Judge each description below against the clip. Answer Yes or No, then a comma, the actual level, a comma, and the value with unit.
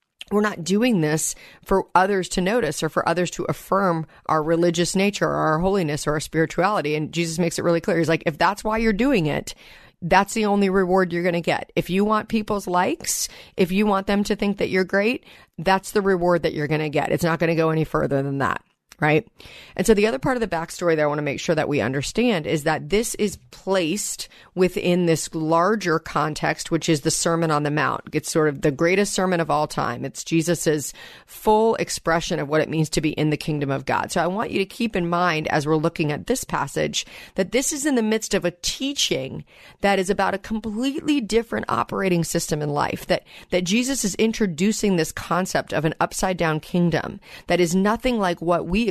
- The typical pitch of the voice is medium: Yes, medium, 175 Hz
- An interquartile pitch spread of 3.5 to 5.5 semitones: Yes, average, 4.1 semitones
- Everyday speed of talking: No, fast, 225 wpm